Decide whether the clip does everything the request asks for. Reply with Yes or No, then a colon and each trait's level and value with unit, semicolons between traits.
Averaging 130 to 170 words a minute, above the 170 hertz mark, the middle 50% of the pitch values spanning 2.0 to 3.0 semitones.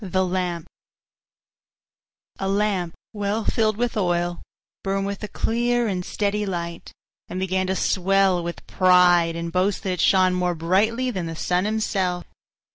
Yes: average, 150 wpm; medium, 185 Hz; narrow, 2.4 semitones